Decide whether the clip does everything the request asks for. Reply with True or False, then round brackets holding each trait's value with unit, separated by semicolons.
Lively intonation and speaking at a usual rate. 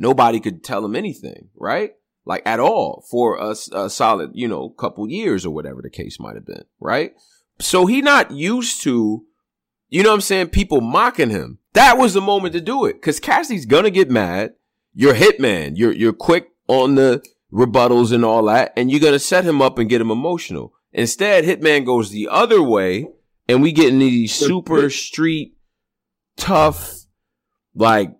True (8.4 semitones; 185 wpm)